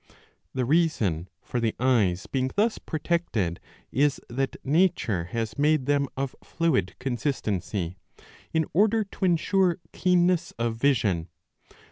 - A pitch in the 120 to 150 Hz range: Yes, low, 135 Hz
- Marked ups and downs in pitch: Yes, wide, 7.2 semitones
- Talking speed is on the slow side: Yes, slow, 120 wpm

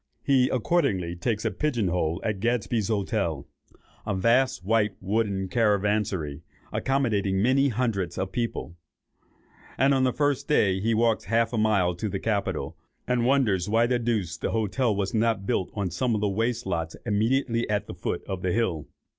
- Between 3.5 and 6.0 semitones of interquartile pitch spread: Yes, average, 3.8 semitones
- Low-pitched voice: Yes, low, 110 Hz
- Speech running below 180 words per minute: Yes, average, 170 wpm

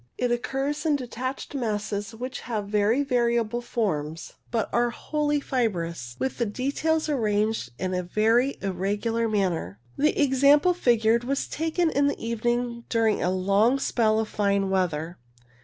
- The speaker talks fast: No, average, 145 wpm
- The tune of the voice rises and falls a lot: No, average, 4.5 semitones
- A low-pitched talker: No, high, 230 Hz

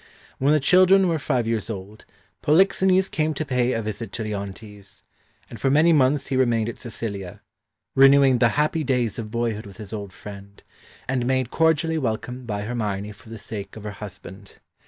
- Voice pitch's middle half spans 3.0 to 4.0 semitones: No, average, 5.1 semitones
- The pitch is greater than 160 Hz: No, low, 120 Hz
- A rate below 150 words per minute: No, average, 180 wpm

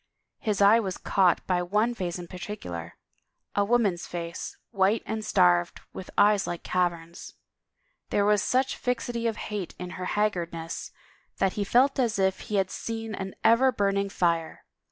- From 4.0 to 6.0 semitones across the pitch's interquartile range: No, average, 3.6 semitones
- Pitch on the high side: Yes, high, 195 Hz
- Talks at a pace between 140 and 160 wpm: No, average, 170 wpm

